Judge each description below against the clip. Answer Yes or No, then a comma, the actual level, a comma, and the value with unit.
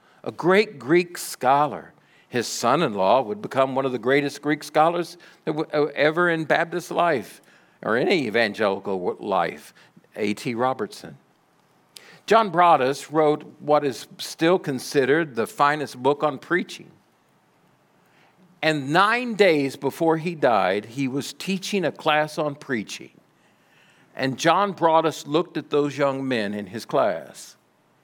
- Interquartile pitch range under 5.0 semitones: Yes, average, 4.0 semitones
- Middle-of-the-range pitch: Yes, medium, 150 Hz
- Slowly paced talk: Yes, slow, 130 wpm